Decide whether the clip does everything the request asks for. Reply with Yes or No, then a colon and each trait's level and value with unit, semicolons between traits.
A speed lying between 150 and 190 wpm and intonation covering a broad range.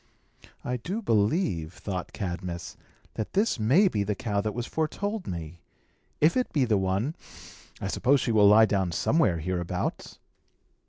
Yes: average, 155 wpm; wide, 8.0 semitones